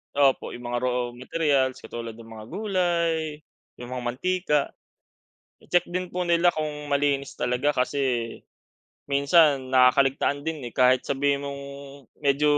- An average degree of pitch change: Yes, average, 3.7 semitones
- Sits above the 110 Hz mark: Yes, medium, 140 Hz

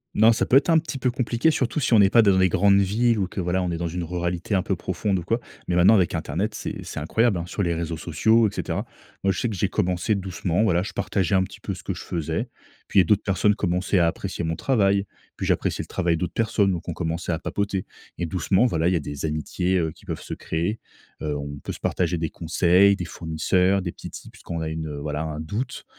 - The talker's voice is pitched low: Yes, very low, 90 Hz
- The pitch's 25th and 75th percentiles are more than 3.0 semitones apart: Yes, average, 3.5 semitones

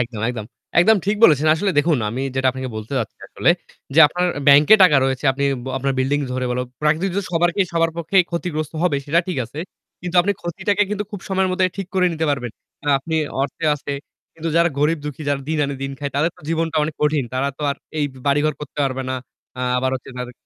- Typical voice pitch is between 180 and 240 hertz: No, medium, 150 Hz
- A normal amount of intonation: Yes, average, 3.9 semitones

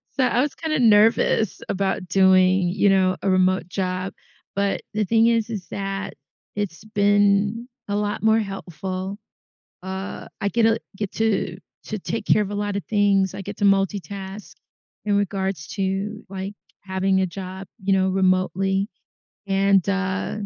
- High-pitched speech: Yes, high, 195 Hz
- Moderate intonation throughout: No, narrow, 1.5 semitones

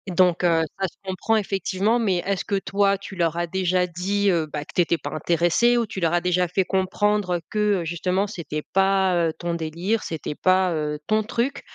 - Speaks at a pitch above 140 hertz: Yes, medium, 185 Hz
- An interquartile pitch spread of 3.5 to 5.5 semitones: No, average, 2.8 semitones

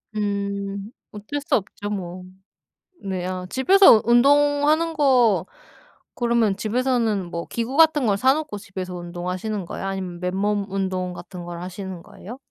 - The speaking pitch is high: Yes, high, 205 Hz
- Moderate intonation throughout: Yes, average, 4.8 semitones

